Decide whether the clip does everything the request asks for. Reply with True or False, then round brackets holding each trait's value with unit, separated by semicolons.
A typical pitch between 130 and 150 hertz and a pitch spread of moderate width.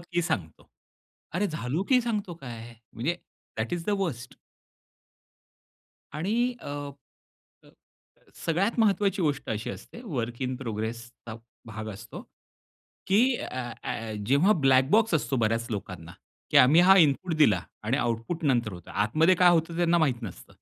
False (135 Hz; 7.2 semitones)